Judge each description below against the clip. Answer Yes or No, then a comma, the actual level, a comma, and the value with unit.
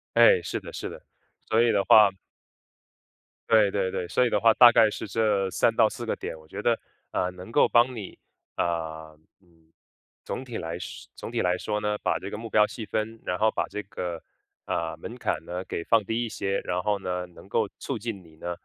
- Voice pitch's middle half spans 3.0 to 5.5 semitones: Yes, average, 4.1 semitones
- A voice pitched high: No, low, 105 Hz